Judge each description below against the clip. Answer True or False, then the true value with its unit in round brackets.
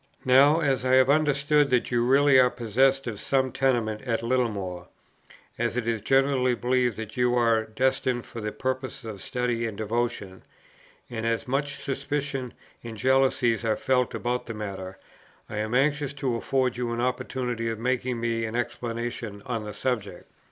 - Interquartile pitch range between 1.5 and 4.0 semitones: True (2.5 semitones)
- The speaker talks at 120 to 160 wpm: False (170 wpm)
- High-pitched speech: False (125 Hz)